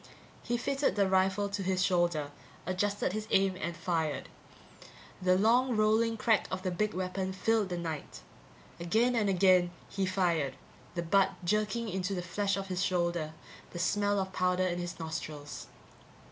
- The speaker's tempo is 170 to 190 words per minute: No, average, 160 wpm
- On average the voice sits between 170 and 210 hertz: Yes, medium, 185 Hz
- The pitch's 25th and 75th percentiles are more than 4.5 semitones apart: No, average, 2.8 semitones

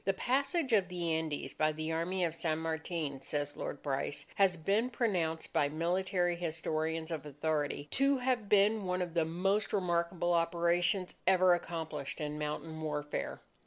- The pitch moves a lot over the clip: No, average, 3.1 semitones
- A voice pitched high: No, medium, 170 Hz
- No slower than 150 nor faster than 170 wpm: Yes, average, 160 wpm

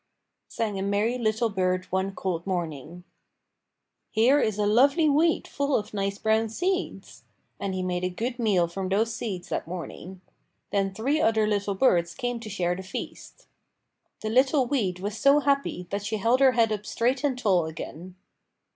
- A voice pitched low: No, high, 210 Hz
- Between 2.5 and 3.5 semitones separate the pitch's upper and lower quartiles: No, average, 4.7 semitones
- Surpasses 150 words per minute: Yes, average, 175 wpm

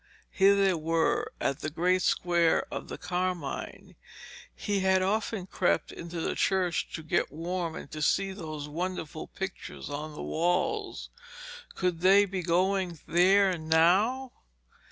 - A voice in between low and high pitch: Yes, medium, 180 Hz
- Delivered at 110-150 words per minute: Yes, average, 140 wpm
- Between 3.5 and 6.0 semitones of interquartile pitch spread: No, average, 2.8 semitones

